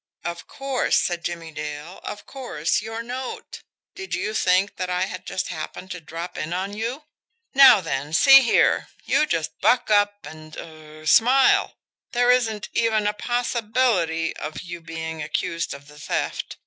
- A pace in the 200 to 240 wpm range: No, average, 160 wpm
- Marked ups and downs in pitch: Yes, wide, 6.3 semitones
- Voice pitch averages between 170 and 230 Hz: Yes, medium, 185 Hz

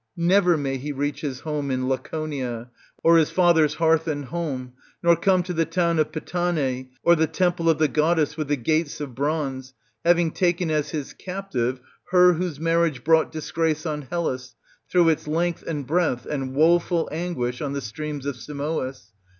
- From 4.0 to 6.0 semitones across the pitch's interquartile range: No, average, 3.4 semitones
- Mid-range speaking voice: Yes, medium, 155 Hz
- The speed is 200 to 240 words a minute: No, average, 175 wpm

